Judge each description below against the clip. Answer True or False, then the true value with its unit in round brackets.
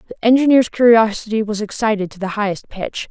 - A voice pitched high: True (215 Hz)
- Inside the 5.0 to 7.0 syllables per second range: True (6.0 syllables/s)